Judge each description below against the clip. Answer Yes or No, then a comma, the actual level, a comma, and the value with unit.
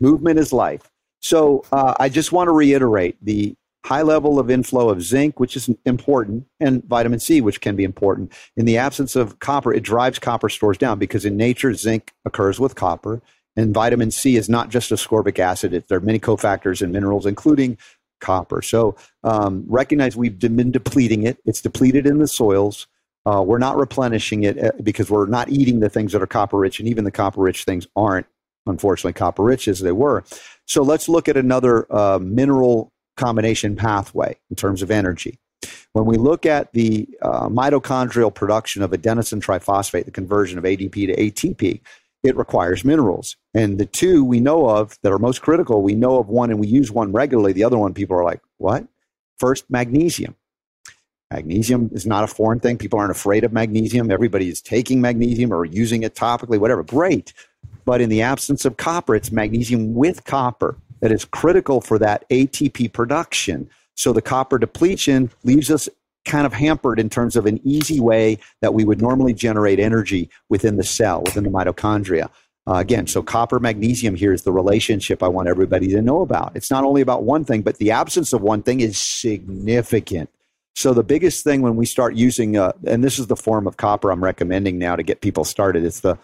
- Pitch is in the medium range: No, low, 115 Hz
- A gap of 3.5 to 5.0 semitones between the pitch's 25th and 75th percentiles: Yes, average, 3.8 semitones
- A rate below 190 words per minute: No, average, 195 wpm